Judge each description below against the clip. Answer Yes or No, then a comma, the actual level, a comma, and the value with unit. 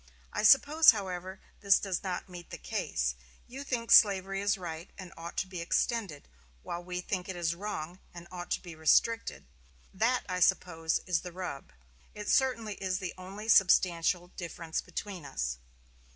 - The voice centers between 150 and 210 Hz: Yes, medium, 185 Hz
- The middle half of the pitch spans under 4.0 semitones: Yes, average, 2.9 semitones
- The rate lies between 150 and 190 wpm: Yes, average, 165 wpm